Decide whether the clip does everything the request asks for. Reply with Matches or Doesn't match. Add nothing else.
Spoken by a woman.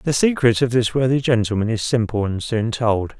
Doesn't match